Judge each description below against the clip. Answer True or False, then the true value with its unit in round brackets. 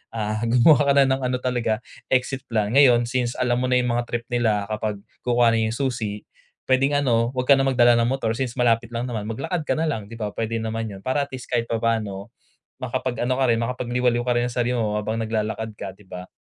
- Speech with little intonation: True (2.3 semitones)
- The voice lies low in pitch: True (120 Hz)